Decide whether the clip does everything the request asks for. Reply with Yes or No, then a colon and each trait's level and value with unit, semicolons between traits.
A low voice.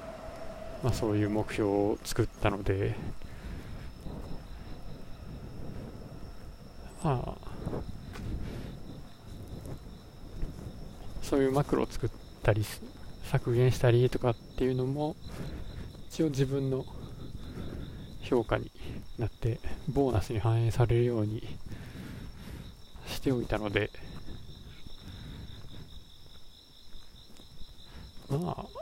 Yes: low, 115 Hz